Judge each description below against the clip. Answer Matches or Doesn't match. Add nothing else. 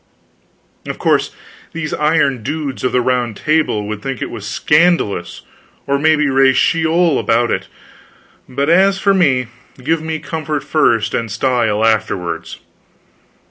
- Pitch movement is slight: Doesn't match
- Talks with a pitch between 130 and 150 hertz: Matches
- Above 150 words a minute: Doesn't match